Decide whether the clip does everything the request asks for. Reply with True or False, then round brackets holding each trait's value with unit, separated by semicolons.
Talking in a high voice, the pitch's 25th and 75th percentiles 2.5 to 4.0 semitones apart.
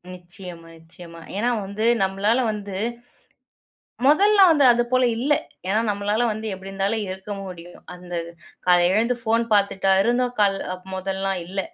True (200 Hz; 3.4 semitones)